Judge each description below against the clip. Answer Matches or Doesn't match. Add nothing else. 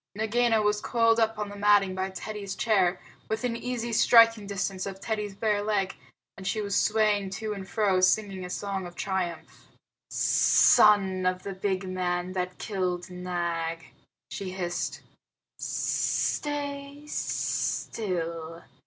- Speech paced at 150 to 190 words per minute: Doesn't match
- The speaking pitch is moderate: Doesn't match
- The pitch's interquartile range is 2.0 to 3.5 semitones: Matches